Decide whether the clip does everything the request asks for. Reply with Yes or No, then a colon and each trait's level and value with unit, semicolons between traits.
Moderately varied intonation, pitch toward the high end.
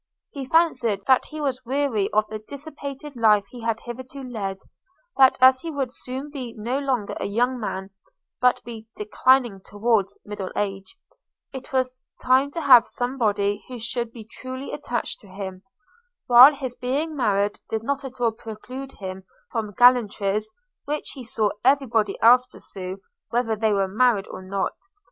Yes: average, 3.9 semitones; high, 240 Hz